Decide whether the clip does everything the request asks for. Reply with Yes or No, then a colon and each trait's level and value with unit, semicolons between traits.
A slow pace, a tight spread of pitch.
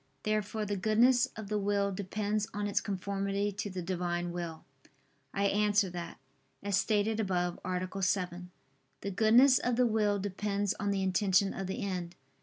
No: average, 165 wpm; narrow, 2.2 semitones